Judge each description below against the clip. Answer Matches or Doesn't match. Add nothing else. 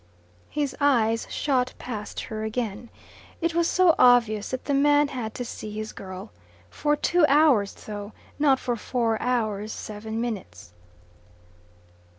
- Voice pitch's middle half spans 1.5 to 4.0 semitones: Doesn't match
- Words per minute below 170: Matches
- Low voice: Doesn't match